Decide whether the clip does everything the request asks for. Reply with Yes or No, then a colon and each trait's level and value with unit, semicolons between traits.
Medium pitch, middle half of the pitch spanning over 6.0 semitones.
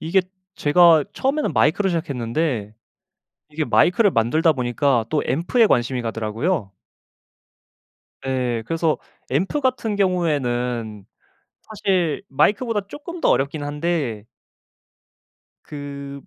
Yes: medium, 150 Hz; wide, 6.7 semitones